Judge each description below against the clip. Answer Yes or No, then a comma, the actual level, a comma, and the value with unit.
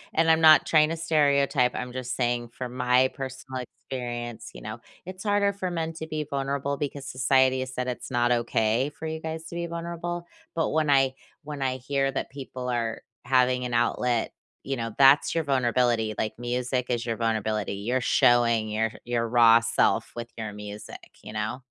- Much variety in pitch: No, average, 3.2 semitones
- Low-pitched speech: Yes, low, 130 Hz